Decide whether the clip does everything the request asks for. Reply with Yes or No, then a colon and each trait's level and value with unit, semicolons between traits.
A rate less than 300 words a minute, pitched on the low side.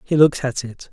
Yes: fast, 260 wpm; low, 130 Hz